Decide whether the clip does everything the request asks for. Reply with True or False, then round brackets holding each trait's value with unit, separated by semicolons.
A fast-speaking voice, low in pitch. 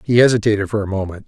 True (235 wpm; 105 Hz)